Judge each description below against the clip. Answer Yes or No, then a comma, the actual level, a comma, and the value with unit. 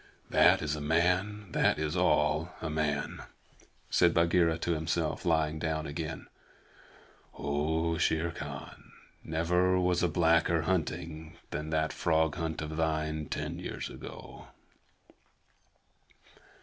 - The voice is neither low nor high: No, very low, 80 Hz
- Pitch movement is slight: Yes, narrow, 1.6 semitones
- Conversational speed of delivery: No, slow, 120 wpm